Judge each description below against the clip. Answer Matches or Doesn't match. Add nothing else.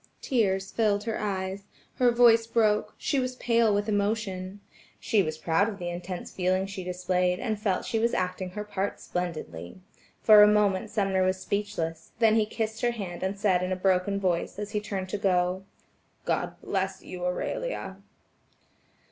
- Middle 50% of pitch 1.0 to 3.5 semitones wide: Matches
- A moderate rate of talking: Matches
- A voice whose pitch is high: Matches